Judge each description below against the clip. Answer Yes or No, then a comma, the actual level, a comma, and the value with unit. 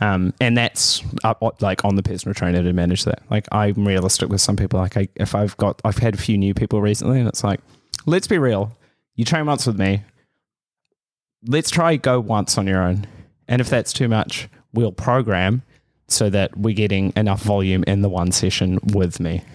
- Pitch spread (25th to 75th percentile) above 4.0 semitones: No, average, 3.6 semitones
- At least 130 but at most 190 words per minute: No, fast, 205 wpm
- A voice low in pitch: Yes, low, 105 Hz